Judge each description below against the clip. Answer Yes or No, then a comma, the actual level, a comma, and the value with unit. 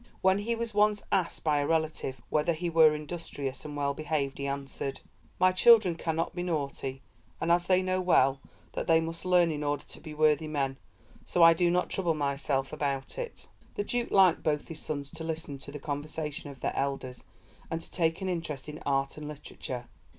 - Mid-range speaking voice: Yes, medium, 155 Hz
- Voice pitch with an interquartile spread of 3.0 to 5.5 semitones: Yes, average, 3.7 semitones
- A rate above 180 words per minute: Yes, average, 200 wpm